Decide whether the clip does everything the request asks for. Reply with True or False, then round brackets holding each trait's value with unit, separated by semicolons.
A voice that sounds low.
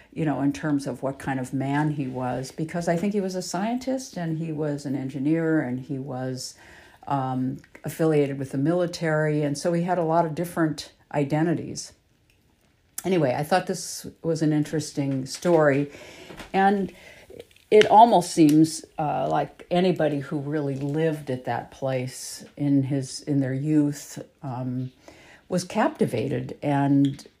False (150 Hz)